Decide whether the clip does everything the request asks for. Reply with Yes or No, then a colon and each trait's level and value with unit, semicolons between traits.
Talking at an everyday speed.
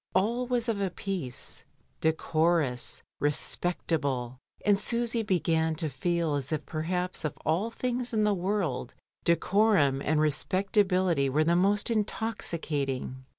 No: slow, 130 wpm